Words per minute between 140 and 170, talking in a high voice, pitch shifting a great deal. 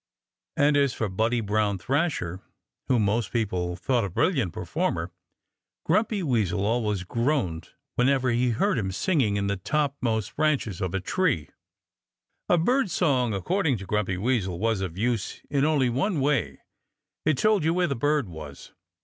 No: average, 160 wpm; low, 120 Hz; wide, 6.9 semitones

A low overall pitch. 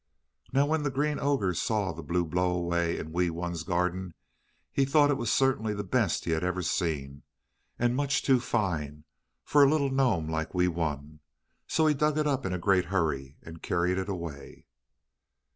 Yes: very low, 90 Hz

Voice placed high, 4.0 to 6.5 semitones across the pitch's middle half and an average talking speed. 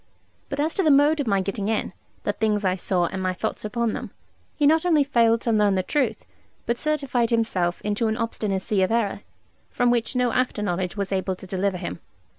No: high, 220 Hz; average, 4.3 semitones; fast, 215 wpm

